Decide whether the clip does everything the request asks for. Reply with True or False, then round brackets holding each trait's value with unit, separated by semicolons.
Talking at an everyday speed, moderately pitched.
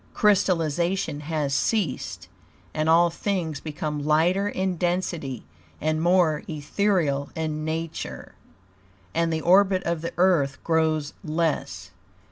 False (110 wpm; 160 Hz)